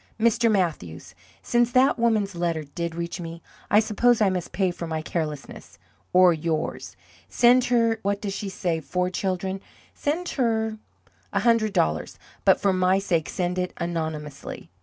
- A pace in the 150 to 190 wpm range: Yes, average, 160 wpm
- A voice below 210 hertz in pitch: Yes, medium, 185 Hz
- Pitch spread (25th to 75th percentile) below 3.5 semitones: No, average, 4.8 semitones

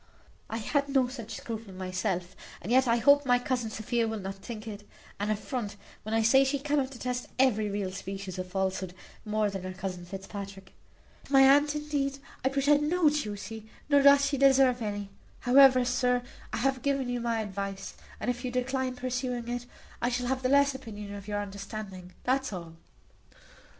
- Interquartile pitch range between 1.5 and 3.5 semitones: No, average, 4.8 semitones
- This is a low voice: No, high, 240 Hz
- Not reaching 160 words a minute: No, average, 185 wpm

